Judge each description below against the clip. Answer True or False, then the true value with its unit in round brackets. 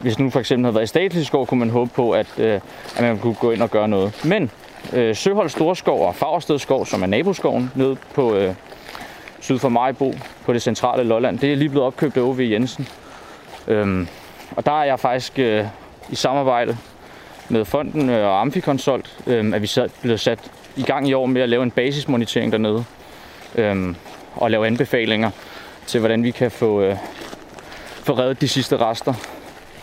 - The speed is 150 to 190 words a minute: True (175 wpm)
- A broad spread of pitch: False (3.1 semitones)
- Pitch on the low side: True (120 Hz)